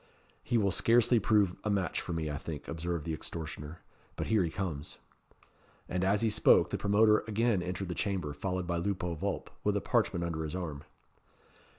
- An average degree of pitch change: Yes, average, 3.8 semitones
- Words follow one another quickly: No, average, 190 wpm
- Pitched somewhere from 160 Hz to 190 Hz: No, very low, 90 Hz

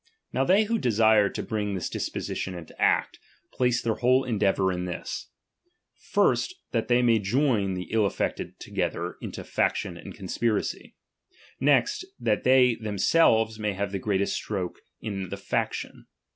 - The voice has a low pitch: Yes, low, 110 Hz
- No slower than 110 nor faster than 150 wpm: Yes, average, 145 wpm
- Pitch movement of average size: Yes, average, 4.0 semitones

